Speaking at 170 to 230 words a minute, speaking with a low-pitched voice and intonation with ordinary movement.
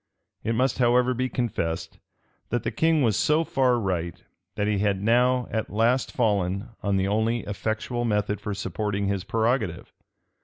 No: average, 160 wpm; low, 110 Hz; average, 3.6 semitones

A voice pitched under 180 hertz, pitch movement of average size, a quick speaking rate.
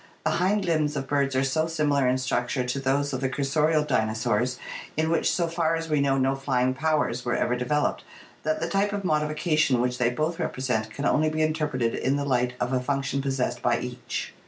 Yes: medium, 140 Hz; average, 3.5 semitones; fast, 210 wpm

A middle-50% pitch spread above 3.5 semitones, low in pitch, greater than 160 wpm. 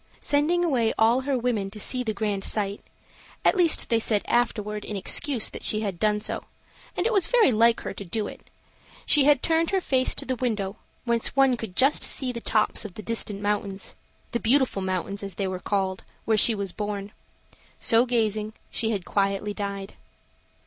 No: average, 3.9 semitones; high, 220 Hz; average, 195 wpm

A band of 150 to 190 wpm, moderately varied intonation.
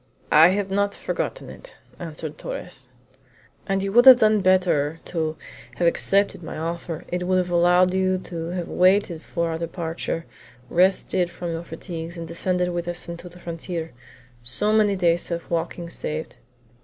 No: average, 165 wpm; narrow, 2.1 semitones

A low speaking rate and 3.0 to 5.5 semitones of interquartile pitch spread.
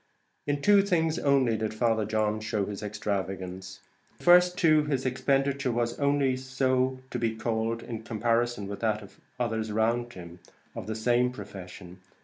No: average, 165 wpm; average, 3.7 semitones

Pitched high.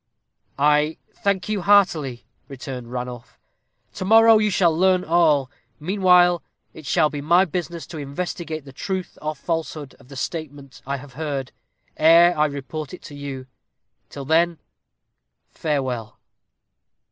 No: medium, 155 Hz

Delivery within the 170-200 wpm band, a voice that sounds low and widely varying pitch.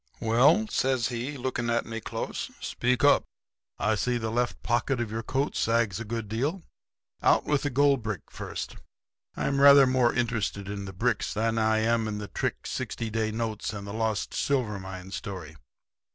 No: average, 180 wpm; low, 115 Hz; average, 2.8 semitones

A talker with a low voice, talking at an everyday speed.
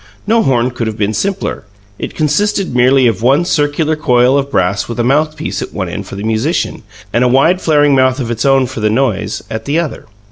No: low, 130 Hz; fast, 220 wpm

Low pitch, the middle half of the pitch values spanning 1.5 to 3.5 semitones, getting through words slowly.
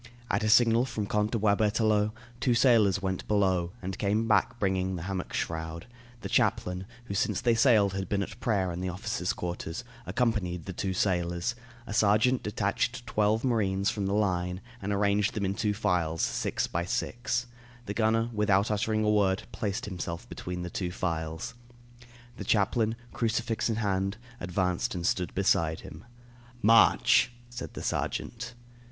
No: low, 100 Hz; average, 3.2 semitones; average, 165 wpm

